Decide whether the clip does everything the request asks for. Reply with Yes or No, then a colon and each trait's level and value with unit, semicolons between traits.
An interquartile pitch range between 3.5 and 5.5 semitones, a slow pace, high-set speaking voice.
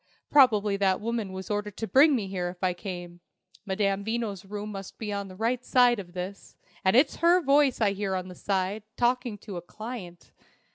No: average, 3.8 semitones; average, 195 wpm; high, 205 Hz